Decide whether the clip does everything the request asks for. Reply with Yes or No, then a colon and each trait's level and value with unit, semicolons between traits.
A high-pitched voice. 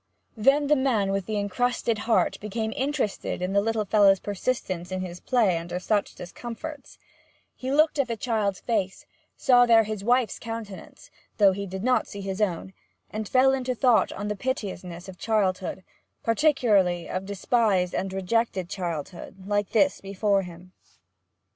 Yes: high, 205 Hz